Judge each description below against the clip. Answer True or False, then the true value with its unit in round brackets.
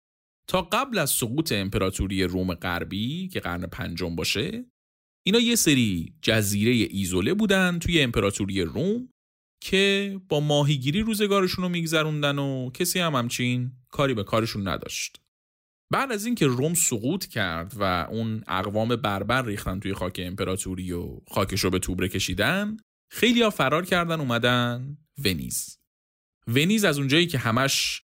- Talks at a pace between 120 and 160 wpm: True (140 wpm)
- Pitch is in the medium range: False (120 Hz)